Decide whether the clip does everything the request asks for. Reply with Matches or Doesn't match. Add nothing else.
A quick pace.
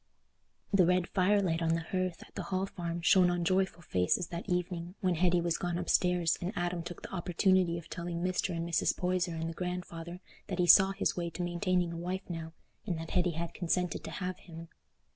Matches